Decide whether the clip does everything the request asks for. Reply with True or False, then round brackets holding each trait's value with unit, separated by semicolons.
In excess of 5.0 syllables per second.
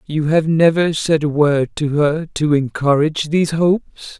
False (4.5 syllables/s)